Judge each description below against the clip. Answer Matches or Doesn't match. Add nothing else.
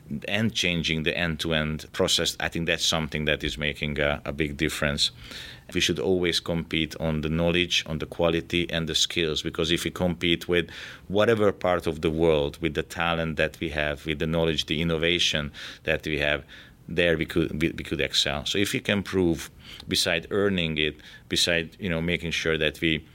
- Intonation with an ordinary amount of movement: Doesn't match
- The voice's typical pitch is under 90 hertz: Matches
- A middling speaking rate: Matches